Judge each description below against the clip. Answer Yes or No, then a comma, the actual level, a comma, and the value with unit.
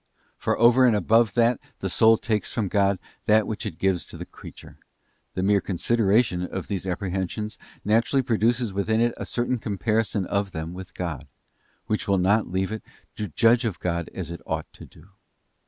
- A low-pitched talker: Yes, low, 105 Hz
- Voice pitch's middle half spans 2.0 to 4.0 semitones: Yes, average, 3.2 semitones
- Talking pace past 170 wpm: Yes, average, 180 wpm